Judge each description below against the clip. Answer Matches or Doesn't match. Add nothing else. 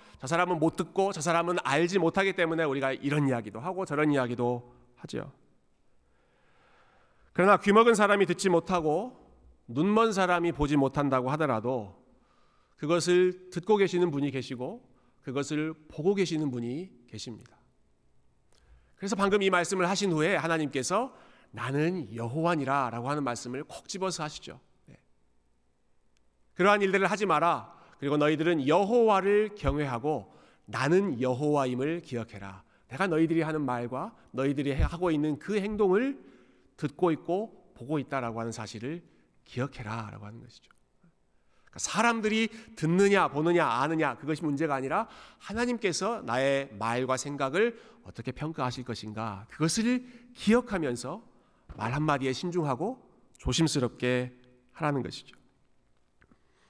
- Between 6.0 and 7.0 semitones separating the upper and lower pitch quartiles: Matches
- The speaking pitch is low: Doesn't match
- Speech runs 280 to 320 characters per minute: Matches